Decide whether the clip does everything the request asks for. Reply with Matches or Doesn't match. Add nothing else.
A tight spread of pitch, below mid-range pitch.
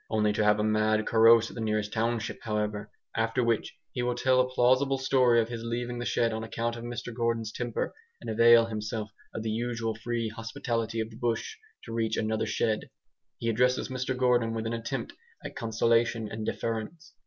Matches